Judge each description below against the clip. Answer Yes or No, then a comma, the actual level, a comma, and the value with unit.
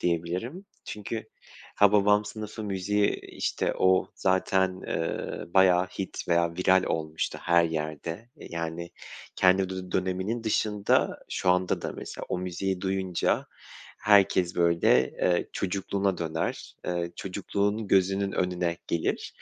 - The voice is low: Yes, very low, 95 Hz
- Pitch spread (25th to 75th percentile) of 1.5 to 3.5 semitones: Yes, narrow, 2.5 semitones